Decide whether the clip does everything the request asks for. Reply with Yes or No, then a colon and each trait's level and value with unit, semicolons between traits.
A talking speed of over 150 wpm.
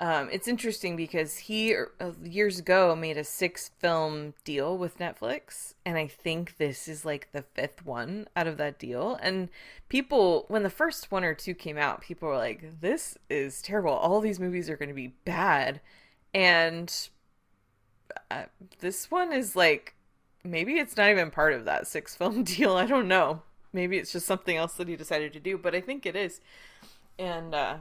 Yes: average, 190 wpm